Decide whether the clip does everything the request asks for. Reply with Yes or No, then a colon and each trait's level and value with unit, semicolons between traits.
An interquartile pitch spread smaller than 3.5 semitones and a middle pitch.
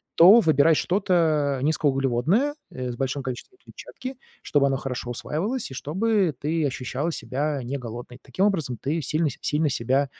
No: average, 4.3 semitones; medium, 145 Hz